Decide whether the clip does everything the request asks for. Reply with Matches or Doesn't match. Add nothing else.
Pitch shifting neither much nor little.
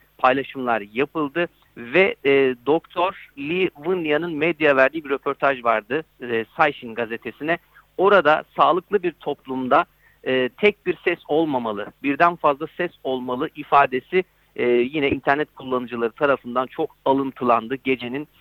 Matches